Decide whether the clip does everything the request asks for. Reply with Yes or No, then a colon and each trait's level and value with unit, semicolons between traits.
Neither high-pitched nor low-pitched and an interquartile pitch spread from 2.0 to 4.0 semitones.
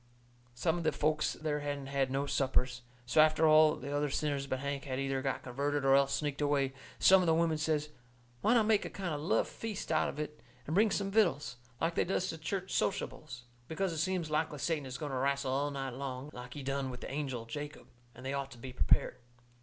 Yes: medium, 145 Hz; average, 2.8 semitones